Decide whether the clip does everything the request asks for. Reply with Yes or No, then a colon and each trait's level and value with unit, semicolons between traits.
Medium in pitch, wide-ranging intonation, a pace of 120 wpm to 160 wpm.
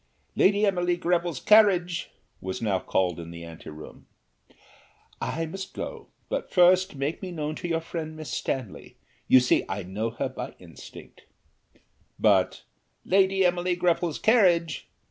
Yes: medium, 170 Hz; wide, 6.6 semitones; average, 140 wpm